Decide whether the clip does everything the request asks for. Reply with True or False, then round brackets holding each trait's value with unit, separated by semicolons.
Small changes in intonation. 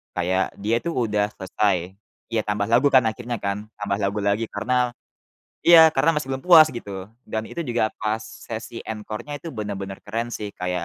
False (3.2 semitones)